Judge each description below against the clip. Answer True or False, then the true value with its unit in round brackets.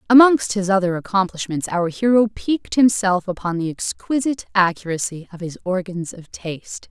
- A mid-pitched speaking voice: False (195 Hz)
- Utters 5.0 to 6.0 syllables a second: True (5.2 syllables/s)